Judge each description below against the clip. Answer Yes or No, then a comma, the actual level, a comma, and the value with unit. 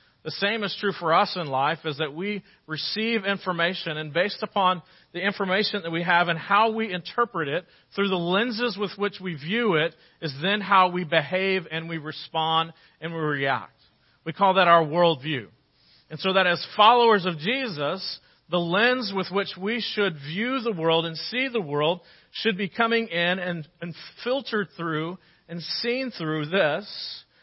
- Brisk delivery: No, average, 180 wpm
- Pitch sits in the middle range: Yes, medium, 180 Hz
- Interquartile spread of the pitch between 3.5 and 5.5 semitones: Yes, average, 4.0 semitones